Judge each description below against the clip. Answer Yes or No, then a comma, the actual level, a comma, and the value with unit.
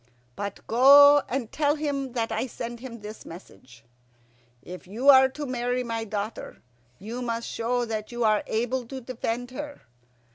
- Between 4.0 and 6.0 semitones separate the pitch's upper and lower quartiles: No, average, 2.9 semitones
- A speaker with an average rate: Yes, average, 160 wpm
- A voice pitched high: Yes, high, 240 Hz